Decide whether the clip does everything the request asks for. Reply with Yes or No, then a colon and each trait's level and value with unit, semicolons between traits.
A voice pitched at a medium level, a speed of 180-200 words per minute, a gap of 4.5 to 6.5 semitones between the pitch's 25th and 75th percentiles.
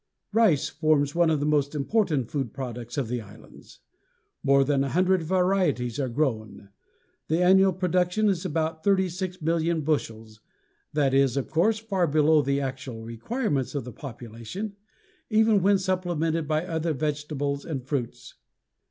No: medium, 155 Hz; average, 145 wpm; average, 5.1 semitones